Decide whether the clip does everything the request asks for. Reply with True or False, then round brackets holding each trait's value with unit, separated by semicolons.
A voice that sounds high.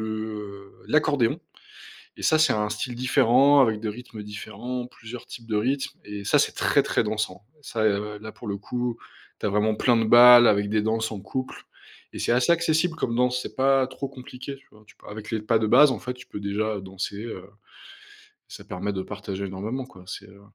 False (110 Hz)